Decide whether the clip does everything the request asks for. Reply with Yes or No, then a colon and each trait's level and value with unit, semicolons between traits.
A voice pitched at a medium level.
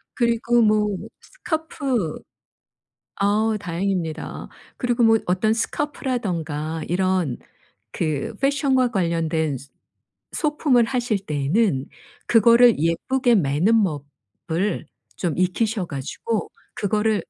No: high, 210 Hz